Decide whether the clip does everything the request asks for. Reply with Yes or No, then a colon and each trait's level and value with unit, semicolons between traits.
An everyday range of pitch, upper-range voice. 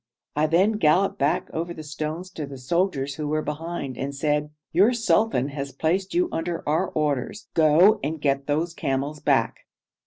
No: average, 3.3 semitones; medium, 155 Hz